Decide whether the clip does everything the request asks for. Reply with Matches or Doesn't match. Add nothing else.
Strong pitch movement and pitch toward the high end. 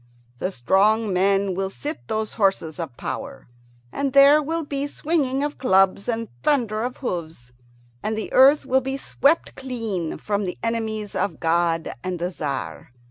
Matches